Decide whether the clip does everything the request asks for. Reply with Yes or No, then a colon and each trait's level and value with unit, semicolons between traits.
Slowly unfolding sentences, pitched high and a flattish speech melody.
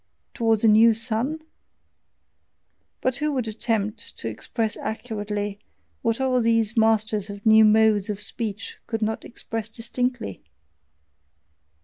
Yes: slow, 120 wpm; high, 220 Hz; narrow, 1.6 semitones